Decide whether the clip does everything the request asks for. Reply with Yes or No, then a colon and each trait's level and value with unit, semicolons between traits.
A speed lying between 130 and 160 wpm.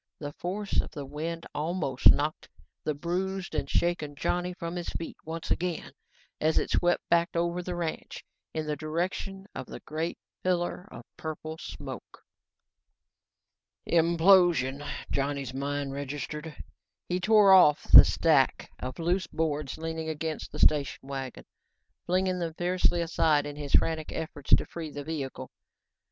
Yes: average, 145 wpm